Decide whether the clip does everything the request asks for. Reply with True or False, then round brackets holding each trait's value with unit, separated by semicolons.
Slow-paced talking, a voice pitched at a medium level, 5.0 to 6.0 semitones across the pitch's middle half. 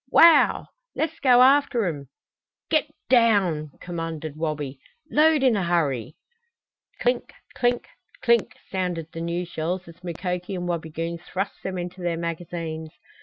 True (130 wpm; 175 Hz; 5.5 semitones)